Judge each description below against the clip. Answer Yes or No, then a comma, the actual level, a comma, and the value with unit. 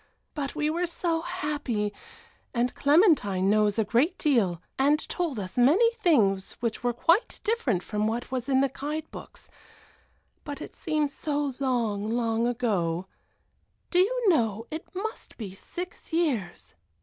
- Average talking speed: Yes, average, 150 wpm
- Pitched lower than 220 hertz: No, very high, 265 Hz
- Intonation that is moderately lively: No, wide, 6.7 semitones